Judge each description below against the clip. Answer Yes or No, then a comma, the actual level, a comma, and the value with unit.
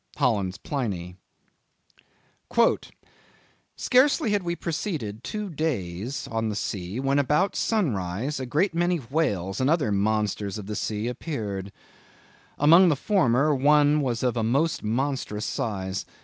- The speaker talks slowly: Yes, slow, 130 wpm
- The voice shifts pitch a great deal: Yes, wide, 7.0 semitones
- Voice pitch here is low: Yes, low, 130 Hz